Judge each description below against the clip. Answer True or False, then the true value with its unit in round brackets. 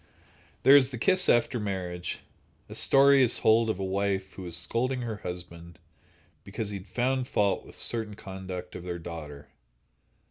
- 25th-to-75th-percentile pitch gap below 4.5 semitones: False (5.0 semitones)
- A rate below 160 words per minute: False (170 wpm)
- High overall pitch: False (100 Hz)